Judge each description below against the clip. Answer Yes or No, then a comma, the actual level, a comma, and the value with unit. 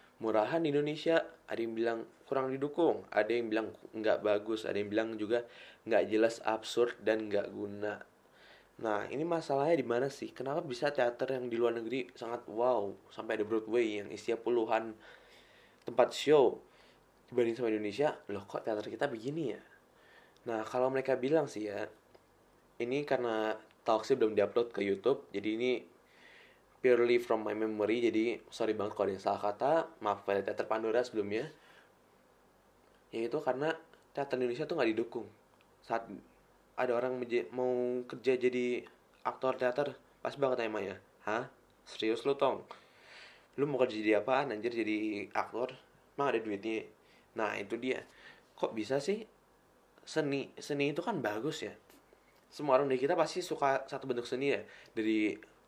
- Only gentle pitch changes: No, average, 3.9 semitones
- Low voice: Yes, low, 120 Hz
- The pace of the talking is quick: Yes, fast, 155 wpm